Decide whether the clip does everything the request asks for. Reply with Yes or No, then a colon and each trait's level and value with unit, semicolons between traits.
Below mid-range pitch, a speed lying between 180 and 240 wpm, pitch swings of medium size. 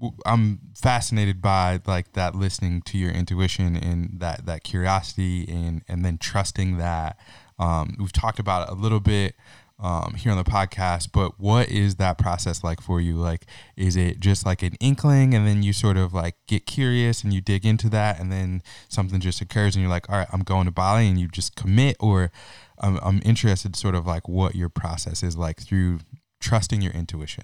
Yes: very low, 95 Hz; fast, 205 wpm; average, 3.0 semitones